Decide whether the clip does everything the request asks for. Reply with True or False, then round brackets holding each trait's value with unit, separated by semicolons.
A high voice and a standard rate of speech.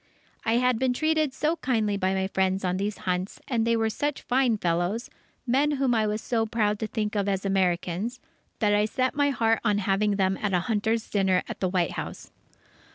False (215 Hz; 210 wpm)